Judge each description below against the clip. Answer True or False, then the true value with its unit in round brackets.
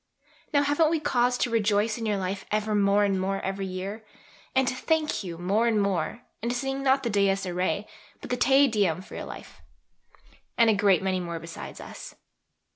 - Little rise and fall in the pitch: False (4.4 semitones)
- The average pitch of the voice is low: False (210 Hz)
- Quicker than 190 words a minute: True (200 wpm)